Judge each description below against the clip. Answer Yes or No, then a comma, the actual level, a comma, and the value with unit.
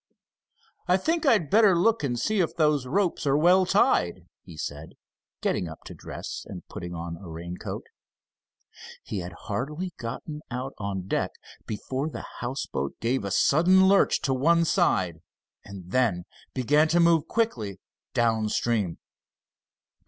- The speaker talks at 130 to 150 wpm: Yes, average, 145 wpm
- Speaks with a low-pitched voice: Yes, low, 130 Hz